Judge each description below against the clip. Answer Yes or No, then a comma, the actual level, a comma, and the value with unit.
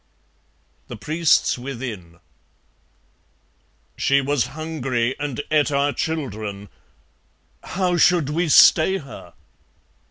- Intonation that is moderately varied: Yes, average, 4.5 semitones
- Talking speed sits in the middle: No, slow, 90 wpm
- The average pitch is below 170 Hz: Yes, medium, 140 Hz